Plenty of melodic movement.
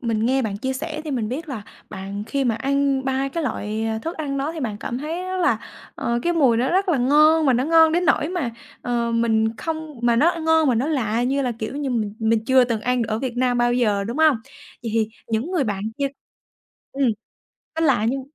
No: average, 4.8 semitones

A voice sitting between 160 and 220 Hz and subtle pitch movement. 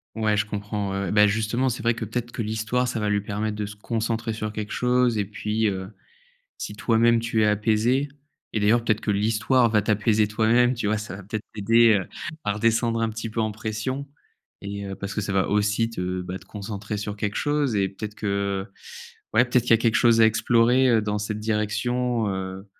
No: low, 110 Hz; narrow, 1.9 semitones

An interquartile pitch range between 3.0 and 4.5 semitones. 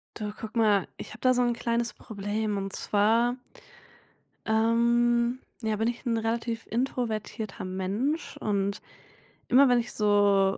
No: narrow, 2.5 semitones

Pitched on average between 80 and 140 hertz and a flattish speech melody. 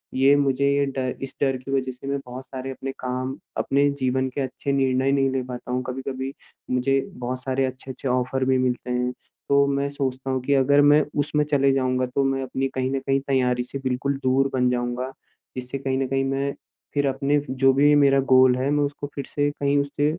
Yes: low, 135 Hz; narrow, 1.3 semitones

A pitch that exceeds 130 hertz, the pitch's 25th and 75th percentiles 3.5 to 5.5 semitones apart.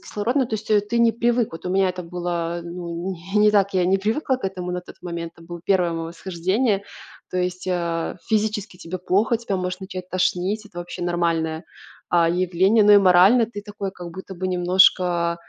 No: medium, 185 Hz; average, 2.9 semitones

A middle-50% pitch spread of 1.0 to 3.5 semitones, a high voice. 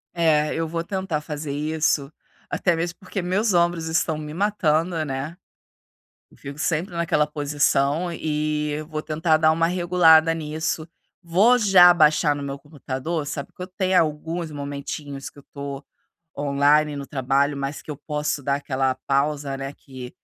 No: average, 2.8 semitones; medium, 155 Hz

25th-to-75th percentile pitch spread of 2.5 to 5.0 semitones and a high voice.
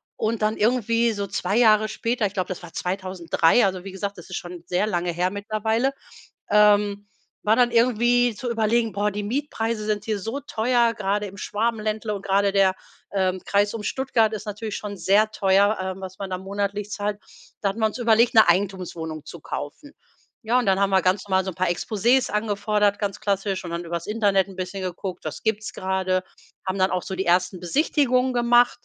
Yes: average, 2.8 semitones; high, 205 Hz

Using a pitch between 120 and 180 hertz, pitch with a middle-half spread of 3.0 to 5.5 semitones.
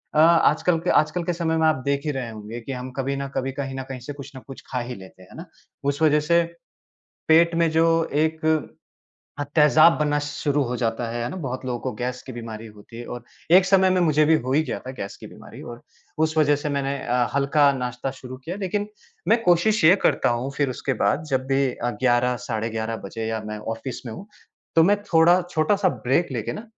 Yes: medium, 140 Hz; average, 4.7 semitones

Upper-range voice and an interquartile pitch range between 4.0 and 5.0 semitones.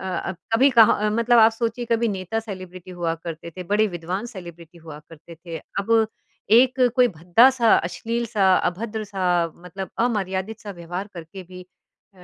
Yes: high, 195 Hz; average, 4.4 semitones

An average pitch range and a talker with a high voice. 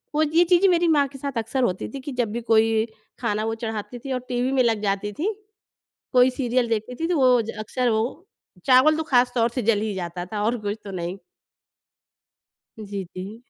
Yes: average, 3.7 semitones; high, 235 Hz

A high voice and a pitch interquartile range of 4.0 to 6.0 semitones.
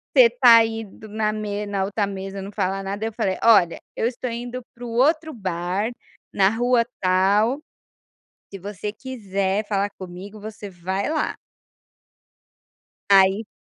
No: high, 205 Hz; average, 2.9 semitones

